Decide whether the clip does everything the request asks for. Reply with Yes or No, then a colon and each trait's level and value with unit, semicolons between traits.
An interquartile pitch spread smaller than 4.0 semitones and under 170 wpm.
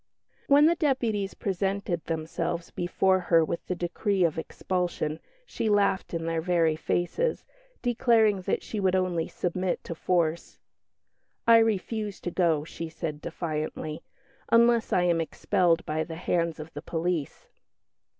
Yes: average, 3.5 semitones; average, 140 wpm